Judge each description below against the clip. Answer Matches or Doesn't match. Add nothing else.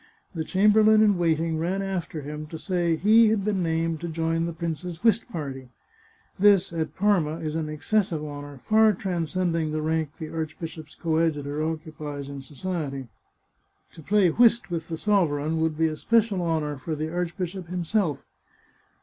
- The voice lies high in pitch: Doesn't match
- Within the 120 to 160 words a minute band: Doesn't match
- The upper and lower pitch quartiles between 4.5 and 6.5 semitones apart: Doesn't match